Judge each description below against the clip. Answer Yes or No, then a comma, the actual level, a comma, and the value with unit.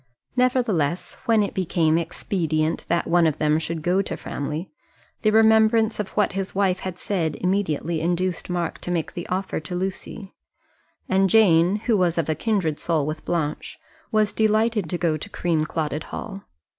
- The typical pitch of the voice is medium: Yes, medium, 180 Hz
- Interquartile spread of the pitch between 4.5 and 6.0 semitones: No, average, 4.0 semitones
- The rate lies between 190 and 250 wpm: No, average, 170 wpm